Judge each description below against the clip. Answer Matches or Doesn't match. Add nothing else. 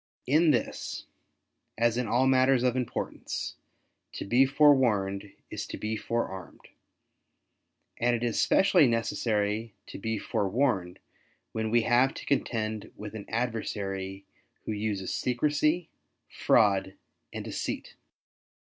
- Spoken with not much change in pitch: Doesn't match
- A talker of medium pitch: Doesn't match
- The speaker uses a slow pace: Matches